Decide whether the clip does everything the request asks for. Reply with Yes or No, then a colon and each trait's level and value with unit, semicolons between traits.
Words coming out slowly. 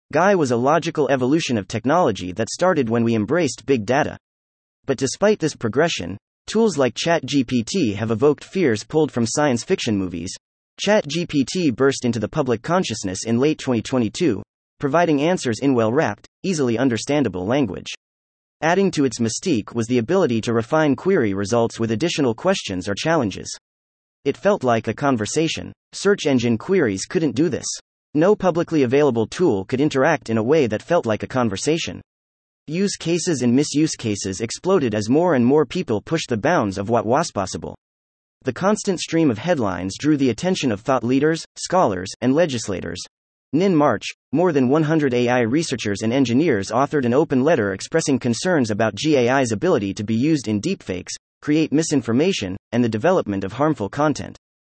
No: average, 165 wpm